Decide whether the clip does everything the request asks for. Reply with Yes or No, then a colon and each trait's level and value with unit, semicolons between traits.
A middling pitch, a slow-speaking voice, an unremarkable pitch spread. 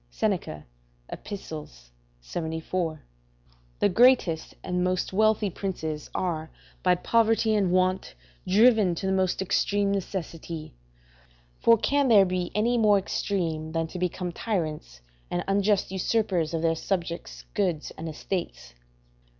Yes: medium, 180 Hz; slow, 125 wpm; average, 3.9 semitones